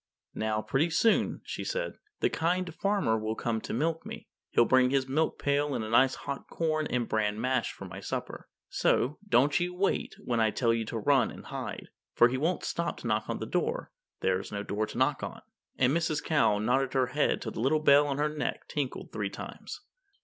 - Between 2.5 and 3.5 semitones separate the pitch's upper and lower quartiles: No, average, 5.2 semitones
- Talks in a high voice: No, low, 130 Hz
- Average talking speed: No, fast, 215 wpm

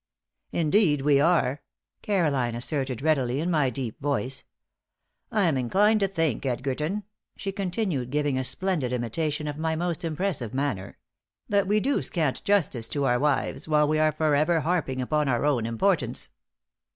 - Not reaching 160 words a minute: Yes, average, 150 wpm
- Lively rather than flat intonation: No, average, 4.8 semitones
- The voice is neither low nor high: Yes, medium, 150 Hz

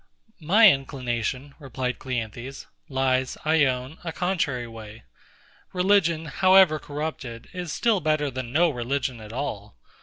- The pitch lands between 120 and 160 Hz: Yes, medium, 140 Hz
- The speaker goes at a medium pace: No, slow, 125 wpm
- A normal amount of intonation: Yes, average, 4.4 semitones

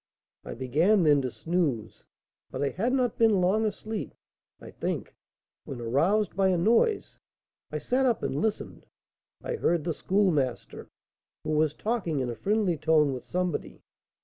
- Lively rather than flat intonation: Yes, wide, 6.7 semitones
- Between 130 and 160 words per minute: Yes, average, 155 wpm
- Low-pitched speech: No, medium, 180 Hz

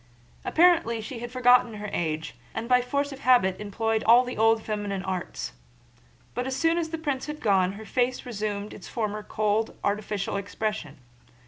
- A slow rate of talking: No, average, 175 wpm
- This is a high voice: Yes, high, 220 Hz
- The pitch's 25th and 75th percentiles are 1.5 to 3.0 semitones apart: No, average, 3.7 semitones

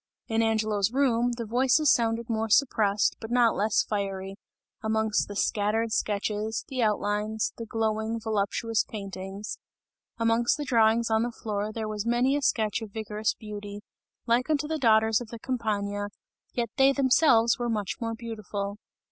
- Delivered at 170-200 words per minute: No, average, 155 wpm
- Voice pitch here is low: No, high, 220 Hz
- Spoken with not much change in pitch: Yes, narrow, 2.0 semitones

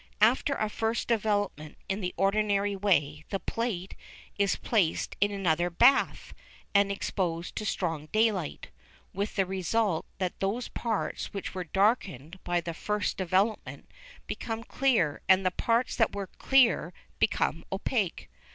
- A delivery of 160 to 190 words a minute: No, average, 140 wpm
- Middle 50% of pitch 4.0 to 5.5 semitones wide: No, average, 3.6 semitones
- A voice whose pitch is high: Yes, high, 195 Hz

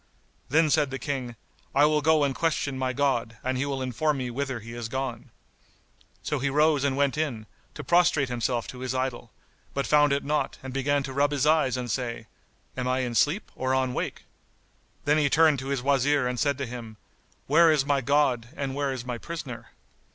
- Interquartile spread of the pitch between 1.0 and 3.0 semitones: Yes, narrow, 2.5 semitones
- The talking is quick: Yes, fast, 210 wpm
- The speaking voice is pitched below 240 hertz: Yes, low, 135 Hz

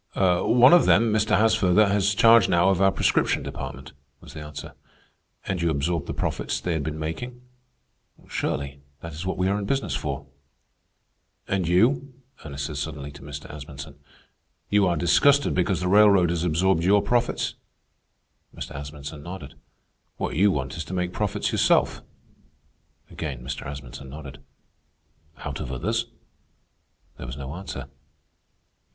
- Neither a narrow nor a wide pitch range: No, wide, 5.7 semitones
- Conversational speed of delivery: Yes, average, 150 wpm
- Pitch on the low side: Yes, very low, 85 Hz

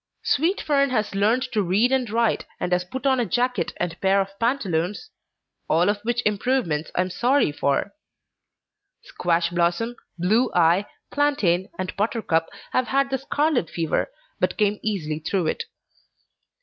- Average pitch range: No, wide, 6.3 semitones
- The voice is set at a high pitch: Yes, high, 205 Hz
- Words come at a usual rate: Yes, average, 155 wpm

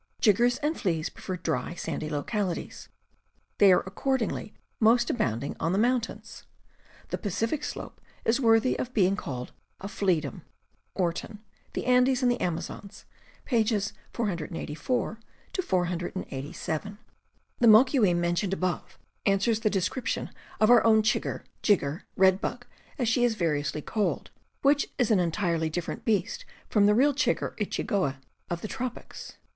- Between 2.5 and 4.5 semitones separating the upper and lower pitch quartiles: No, wide, 5.4 semitones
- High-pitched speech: Yes, high, 205 Hz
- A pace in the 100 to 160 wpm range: Yes, average, 150 wpm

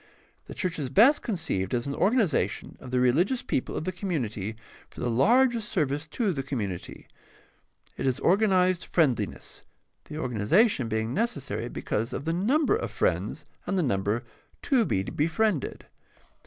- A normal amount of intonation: No, wide, 8.7 semitones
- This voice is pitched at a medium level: Yes, medium, 155 Hz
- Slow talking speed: No, average, 155 wpm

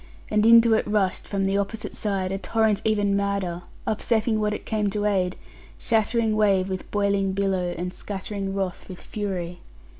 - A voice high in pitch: Yes, high, 200 Hz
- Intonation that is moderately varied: No, narrow, 2.0 semitones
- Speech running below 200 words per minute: Yes, average, 170 wpm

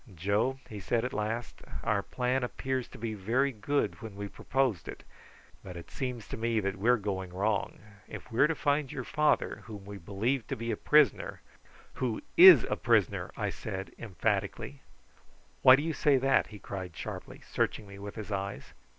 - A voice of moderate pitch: No, low, 110 Hz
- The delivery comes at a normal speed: Yes, average, 195 wpm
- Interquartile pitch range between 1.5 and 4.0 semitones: No, average, 4.5 semitones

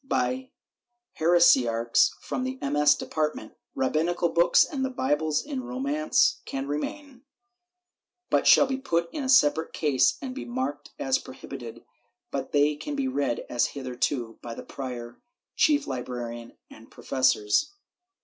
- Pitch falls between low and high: Yes, medium, 150 Hz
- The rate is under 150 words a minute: Yes, slow, 135 wpm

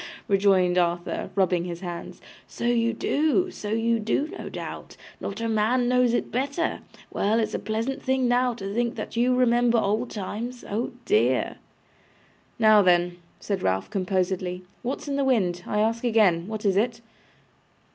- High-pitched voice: Yes, high, 220 Hz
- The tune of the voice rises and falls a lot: No, average, 4.3 semitones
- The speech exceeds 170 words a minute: No, average, 165 wpm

